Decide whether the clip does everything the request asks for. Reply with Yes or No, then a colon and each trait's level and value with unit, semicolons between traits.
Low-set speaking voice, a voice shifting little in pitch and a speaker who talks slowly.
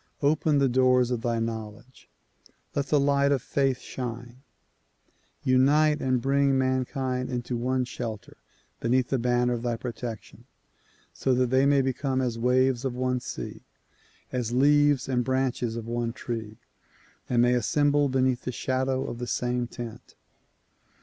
No: low, 125 Hz; narrow, 1.7 semitones; average, 150 wpm